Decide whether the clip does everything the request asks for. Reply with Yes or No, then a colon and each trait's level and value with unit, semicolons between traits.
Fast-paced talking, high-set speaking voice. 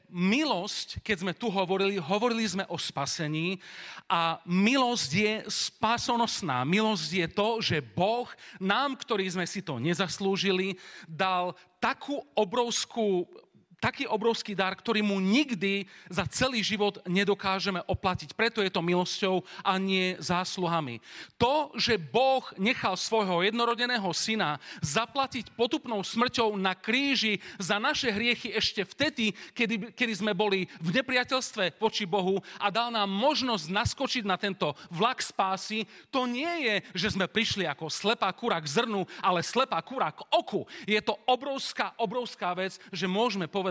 No: average, 140 wpm; high, 205 Hz